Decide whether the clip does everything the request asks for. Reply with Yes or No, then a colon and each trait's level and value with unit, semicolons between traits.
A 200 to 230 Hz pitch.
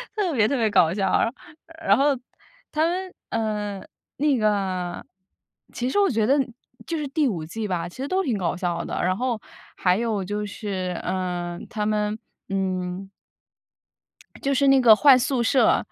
Yes: high, 215 Hz